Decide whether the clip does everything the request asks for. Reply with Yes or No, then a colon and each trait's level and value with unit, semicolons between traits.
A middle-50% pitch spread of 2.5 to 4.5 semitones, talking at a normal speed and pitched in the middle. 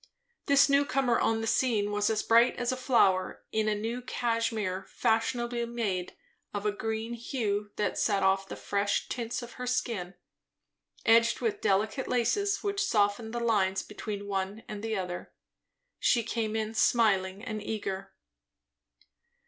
No: average, 2.8 semitones; average, 155 wpm; high, 220 Hz